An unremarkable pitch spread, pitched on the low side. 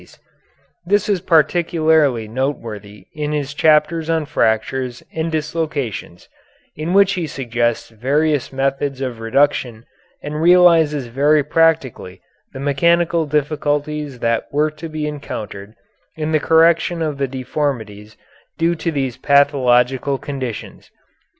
No: average, 4.0 semitones; medium, 145 Hz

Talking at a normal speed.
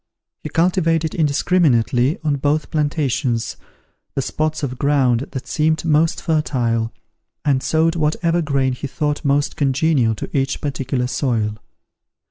No: slow, 125 wpm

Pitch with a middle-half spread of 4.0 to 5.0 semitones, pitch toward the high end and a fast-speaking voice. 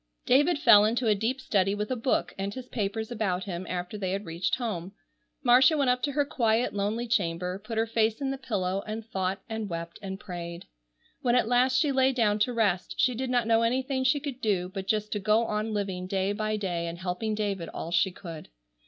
Yes: average, 4.3 semitones; high, 215 Hz; fast, 225 wpm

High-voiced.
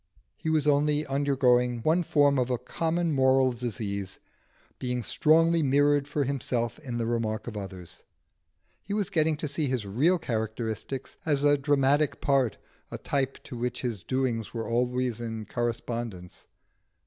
No: low, 130 Hz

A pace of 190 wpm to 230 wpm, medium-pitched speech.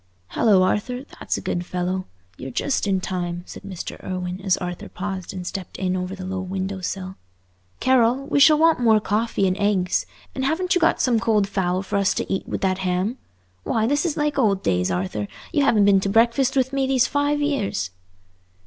No: fast, 205 wpm; high, 195 Hz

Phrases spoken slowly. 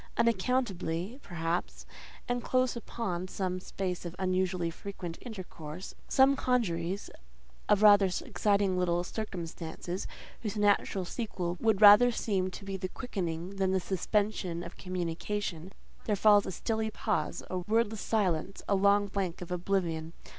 Yes: slow, 130 wpm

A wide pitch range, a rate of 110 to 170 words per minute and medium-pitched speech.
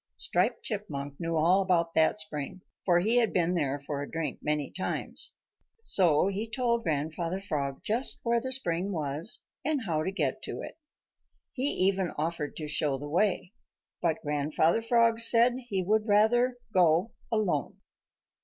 Yes: wide, 6.1 semitones; average, 165 wpm; medium, 180 Hz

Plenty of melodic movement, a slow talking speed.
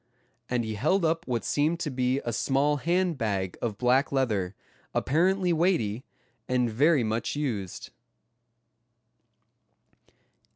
Yes: wide, 5.8 semitones; slow, 120 wpm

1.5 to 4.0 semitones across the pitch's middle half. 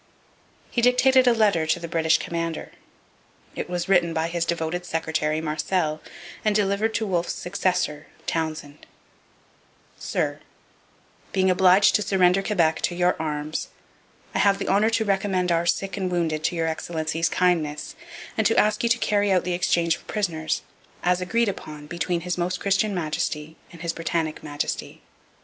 Yes: average, 3.4 semitones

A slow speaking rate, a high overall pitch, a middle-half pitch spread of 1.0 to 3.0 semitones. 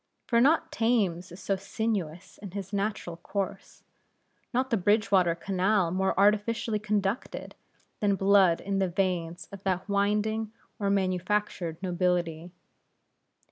Yes: slow, 125 wpm; high, 195 Hz; narrow, 2.5 semitones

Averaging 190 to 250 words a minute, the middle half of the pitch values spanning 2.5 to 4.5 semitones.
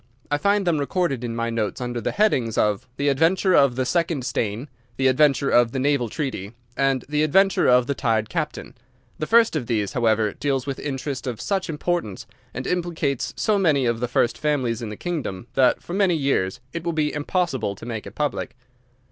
No: average, 200 wpm; average, 5.2 semitones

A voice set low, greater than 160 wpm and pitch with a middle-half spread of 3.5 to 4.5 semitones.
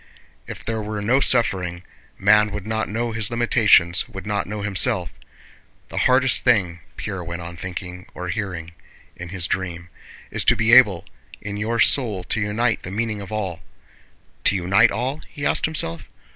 Yes: low, 105 Hz; average, 170 wpm; average, 4.0 semitones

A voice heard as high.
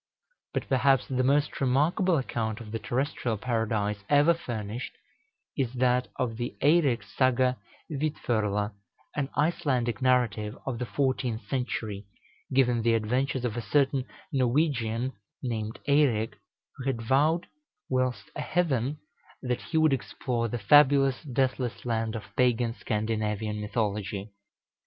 No: low, 125 Hz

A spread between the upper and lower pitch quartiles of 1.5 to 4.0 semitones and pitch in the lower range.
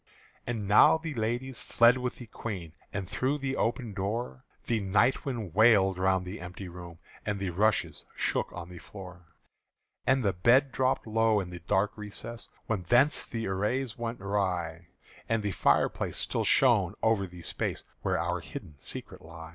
No: average, 4.5 semitones; low, 105 Hz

